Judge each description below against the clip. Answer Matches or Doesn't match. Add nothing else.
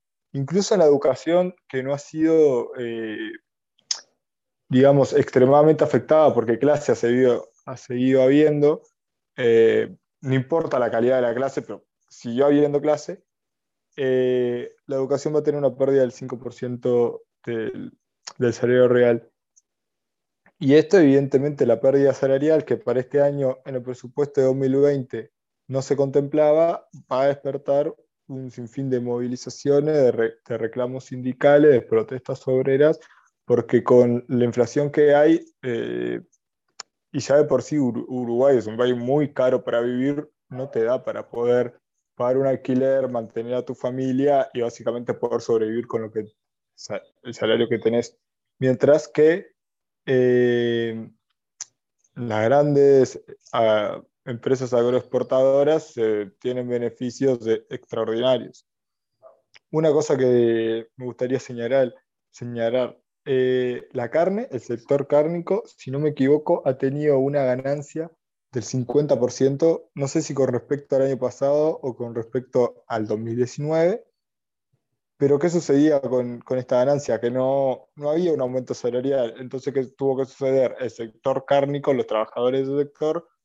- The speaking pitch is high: Doesn't match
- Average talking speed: Matches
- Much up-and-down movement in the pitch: Doesn't match